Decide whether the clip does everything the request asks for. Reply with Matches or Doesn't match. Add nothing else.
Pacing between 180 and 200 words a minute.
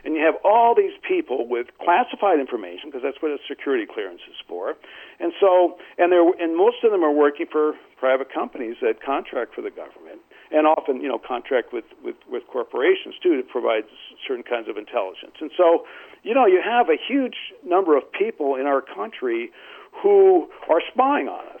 Matches